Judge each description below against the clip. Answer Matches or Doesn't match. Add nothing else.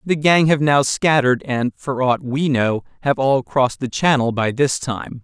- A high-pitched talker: Doesn't match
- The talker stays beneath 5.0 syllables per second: Matches